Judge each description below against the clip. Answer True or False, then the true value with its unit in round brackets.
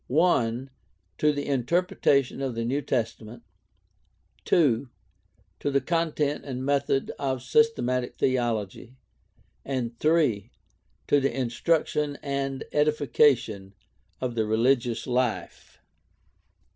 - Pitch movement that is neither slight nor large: True (3.3 semitones)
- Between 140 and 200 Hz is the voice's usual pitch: False (130 Hz)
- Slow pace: True (105 wpm)